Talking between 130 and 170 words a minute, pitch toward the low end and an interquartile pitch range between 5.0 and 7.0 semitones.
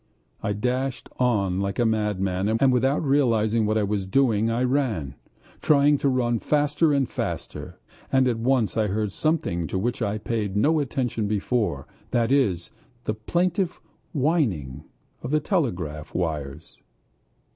Yes: average, 150 wpm; low, 115 Hz; average, 5.3 semitones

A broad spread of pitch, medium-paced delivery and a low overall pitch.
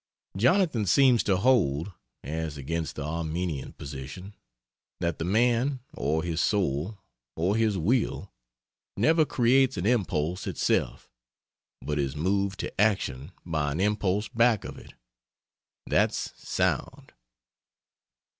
No: wide, 6.3 semitones; slow, 115 wpm; very low, 95 Hz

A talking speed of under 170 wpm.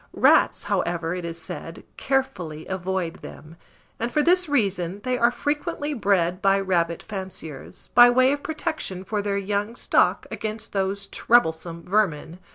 Yes: average, 150 wpm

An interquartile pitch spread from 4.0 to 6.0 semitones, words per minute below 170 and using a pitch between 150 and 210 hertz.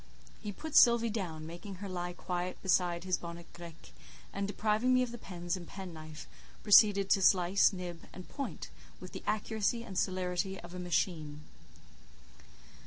No: average, 3.0 semitones; average, 160 wpm; medium, 185 Hz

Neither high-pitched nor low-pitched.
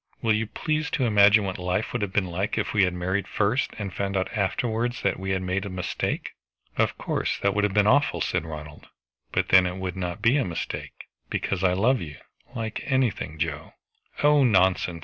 No: low, 100 Hz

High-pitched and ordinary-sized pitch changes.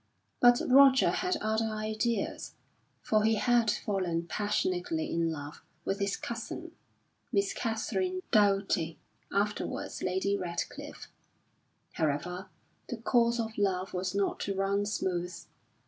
Yes: high, 205 Hz; average, 3.5 semitones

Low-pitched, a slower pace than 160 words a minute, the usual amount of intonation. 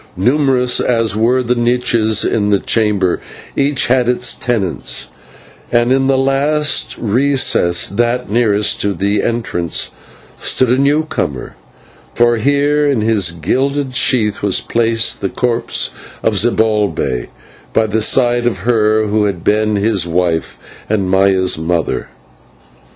Yes: low, 115 Hz; slow, 135 wpm; average, 3.8 semitones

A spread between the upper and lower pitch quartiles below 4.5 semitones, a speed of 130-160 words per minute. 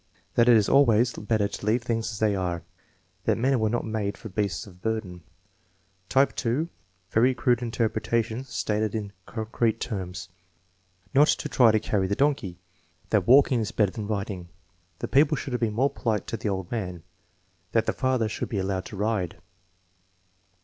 No: average, 3.2 semitones; average, 175 wpm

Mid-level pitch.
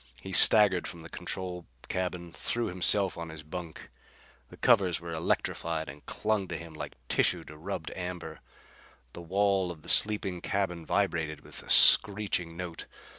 No: very low, 90 Hz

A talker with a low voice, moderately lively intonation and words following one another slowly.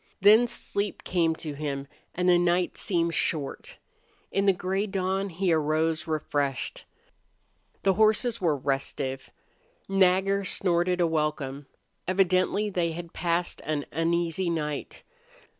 No: medium, 175 Hz; average, 3.6 semitones; slow, 125 wpm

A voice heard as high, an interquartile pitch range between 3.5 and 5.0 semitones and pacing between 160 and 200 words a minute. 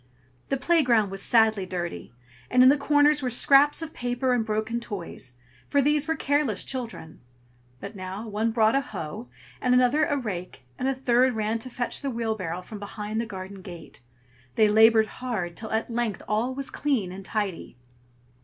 Yes: high, 225 Hz; average, 4.1 semitones; average, 180 wpm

